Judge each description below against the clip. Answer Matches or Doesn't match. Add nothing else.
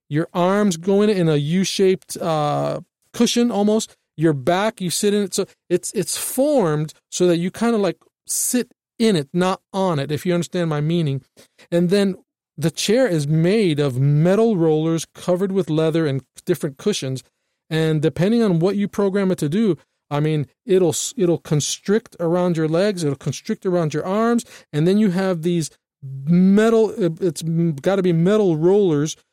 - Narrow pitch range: Doesn't match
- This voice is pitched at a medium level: Matches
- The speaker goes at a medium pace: Matches